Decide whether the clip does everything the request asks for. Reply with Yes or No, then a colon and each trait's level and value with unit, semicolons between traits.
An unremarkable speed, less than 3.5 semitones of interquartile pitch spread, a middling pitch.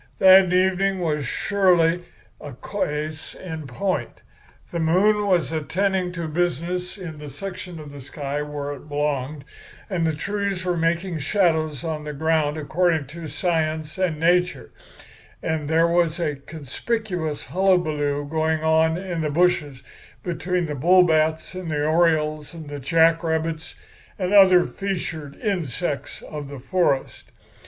Yes: average, 145 wpm; average, 3.1 semitones; medium, 160 Hz